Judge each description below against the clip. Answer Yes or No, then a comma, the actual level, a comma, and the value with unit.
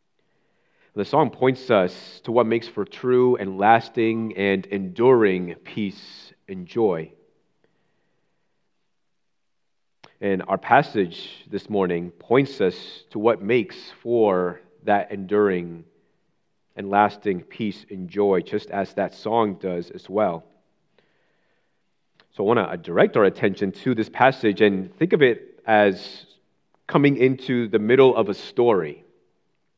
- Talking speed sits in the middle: No, slow, 125 wpm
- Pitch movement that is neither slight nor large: Yes, average, 3.1 semitones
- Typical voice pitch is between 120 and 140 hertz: No, low, 105 Hz